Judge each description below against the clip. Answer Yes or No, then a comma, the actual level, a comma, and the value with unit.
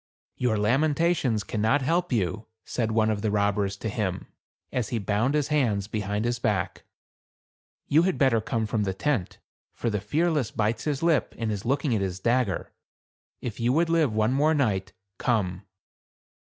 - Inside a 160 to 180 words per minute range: Yes, average, 170 wpm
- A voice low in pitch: Yes, low, 115 Hz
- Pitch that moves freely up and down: No, average, 5.0 semitones